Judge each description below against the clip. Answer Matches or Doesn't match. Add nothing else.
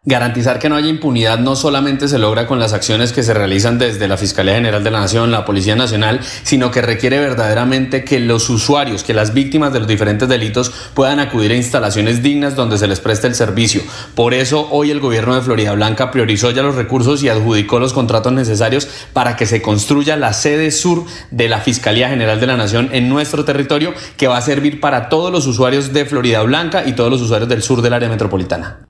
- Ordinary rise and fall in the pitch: Matches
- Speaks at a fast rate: Matches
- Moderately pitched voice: Doesn't match